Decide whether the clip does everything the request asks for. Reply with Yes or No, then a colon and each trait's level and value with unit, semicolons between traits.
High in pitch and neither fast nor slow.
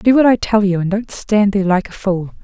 No: high, 205 Hz; fast, 295 wpm